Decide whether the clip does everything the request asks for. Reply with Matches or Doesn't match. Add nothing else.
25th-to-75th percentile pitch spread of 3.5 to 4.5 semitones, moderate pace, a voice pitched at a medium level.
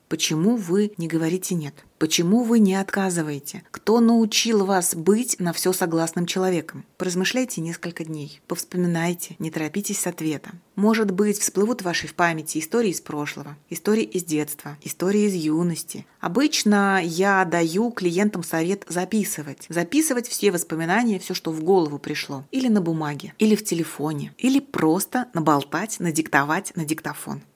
Matches